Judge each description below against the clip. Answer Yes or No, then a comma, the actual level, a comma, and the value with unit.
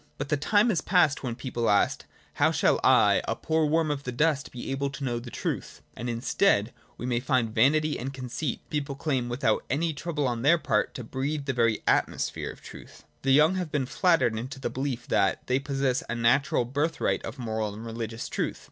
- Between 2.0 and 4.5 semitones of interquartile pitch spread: Yes, average, 3.8 semitones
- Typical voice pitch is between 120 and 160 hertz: Yes, low, 135 Hz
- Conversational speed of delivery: No, fast, 215 wpm